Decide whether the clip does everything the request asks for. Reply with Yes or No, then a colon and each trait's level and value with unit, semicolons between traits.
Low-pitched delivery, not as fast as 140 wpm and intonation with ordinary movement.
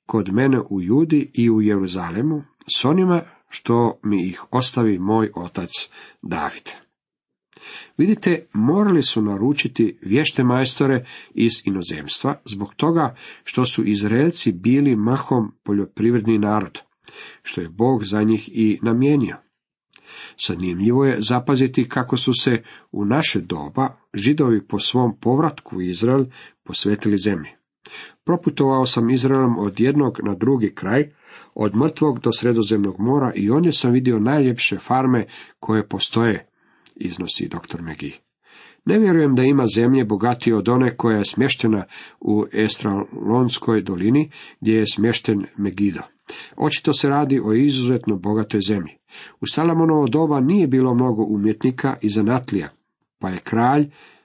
Yes: low, 120 Hz; average, 130 wpm; average, 4.2 semitones